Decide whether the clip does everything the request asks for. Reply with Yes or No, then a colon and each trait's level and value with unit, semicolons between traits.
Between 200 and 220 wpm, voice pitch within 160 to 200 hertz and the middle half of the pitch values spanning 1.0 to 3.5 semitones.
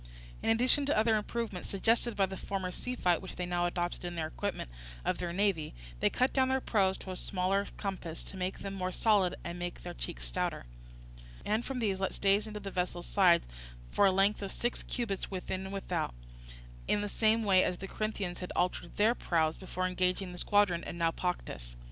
Yes: fast, 205 wpm; high, 190 Hz; average, 2.8 semitones